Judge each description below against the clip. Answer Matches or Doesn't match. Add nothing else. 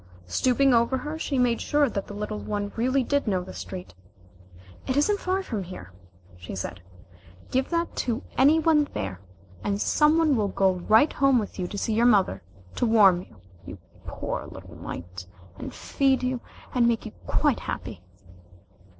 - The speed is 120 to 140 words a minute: Doesn't match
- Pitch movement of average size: Doesn't match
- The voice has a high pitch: Matches